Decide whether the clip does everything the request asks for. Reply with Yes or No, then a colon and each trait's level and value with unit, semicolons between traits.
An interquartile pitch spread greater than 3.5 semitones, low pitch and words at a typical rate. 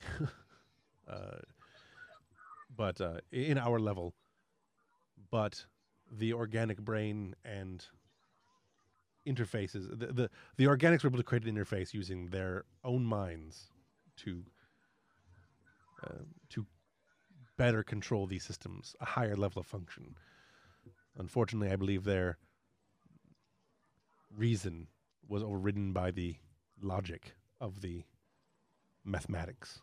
No: average, 4.1 semitones; low, 105 Hz; slow, 105 wpm